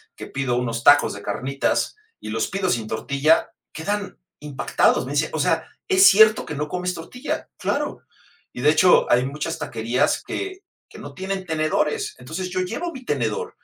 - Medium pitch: Yes, medium, 160 Hz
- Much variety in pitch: Yes, wide, 6.7 semitones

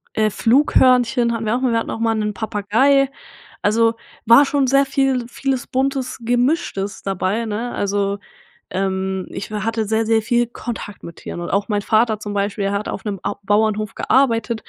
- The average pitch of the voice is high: Yes, high, 225 Hz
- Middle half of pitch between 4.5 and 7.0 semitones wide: No, average, 3.0 semitones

